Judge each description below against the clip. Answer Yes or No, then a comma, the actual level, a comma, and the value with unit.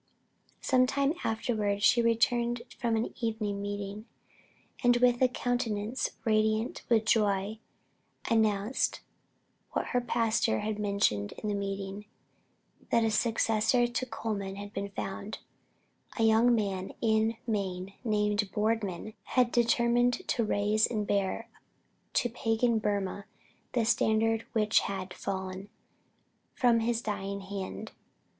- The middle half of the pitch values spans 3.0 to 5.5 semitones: No, narrow, 2.5 semitones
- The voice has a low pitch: No, high, 220 Hz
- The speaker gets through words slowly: Yes, slow, 125 wpm